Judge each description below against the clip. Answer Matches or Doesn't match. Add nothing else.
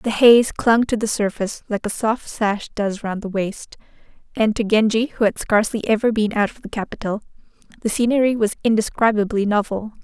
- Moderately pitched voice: Doesn't match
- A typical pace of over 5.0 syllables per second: Matches